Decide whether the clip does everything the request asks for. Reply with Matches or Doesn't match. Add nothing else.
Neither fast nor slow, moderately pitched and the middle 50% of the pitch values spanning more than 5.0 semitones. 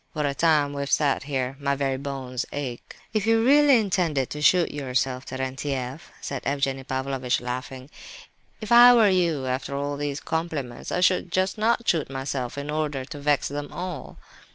Doesn't match